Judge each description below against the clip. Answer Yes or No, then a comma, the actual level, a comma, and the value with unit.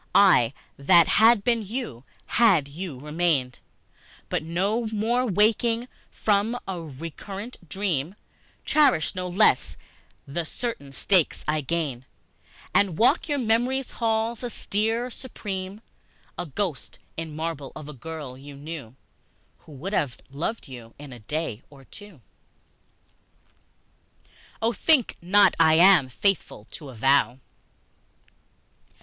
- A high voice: No, medium, 175 Hz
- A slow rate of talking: Yes, slow, 125 wpm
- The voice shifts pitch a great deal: Yes, wide, 7.3 semitones